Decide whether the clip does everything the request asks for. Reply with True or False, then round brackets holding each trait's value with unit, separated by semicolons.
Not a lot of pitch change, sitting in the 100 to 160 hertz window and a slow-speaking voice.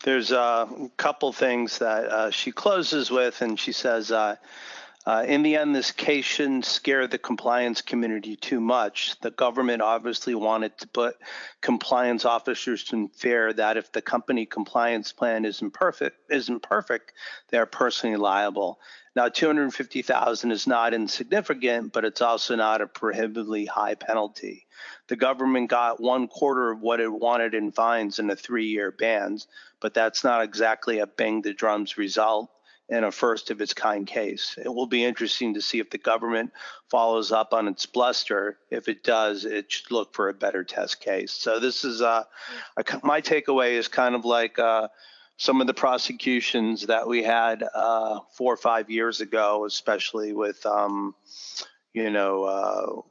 False (2.0 semitones; 115 Hz; 170 wpm)